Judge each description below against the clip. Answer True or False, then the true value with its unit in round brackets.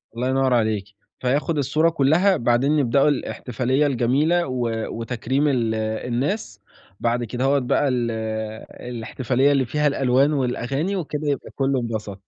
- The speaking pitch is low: True (130 Hz)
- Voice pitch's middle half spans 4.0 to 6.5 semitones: False (3.3 semitones)